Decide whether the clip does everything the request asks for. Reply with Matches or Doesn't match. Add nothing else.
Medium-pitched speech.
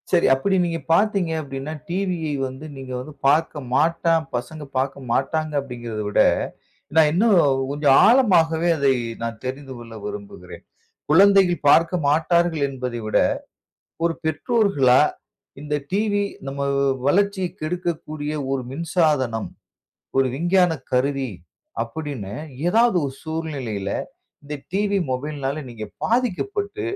Matches